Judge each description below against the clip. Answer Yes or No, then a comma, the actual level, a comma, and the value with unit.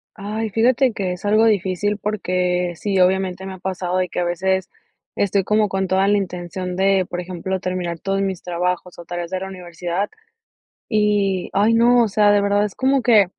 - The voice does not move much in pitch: Yes, narrow, 2.3 semitones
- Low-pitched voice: No, high, 190 Hz